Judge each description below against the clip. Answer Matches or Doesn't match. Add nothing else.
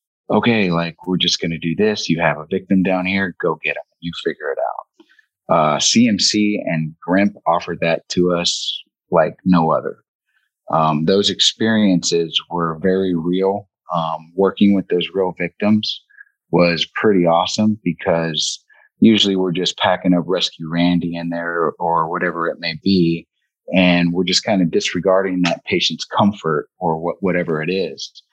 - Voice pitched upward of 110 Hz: Doesn't match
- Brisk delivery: Doesn't match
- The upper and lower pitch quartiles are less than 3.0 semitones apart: Matches